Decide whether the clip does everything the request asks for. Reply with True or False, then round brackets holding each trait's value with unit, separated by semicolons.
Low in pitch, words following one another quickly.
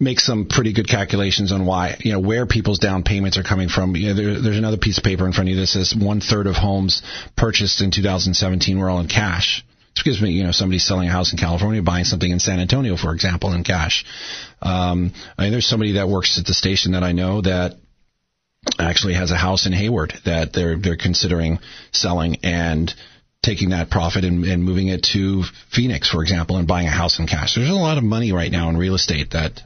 True (95 Hz; 235 wpm)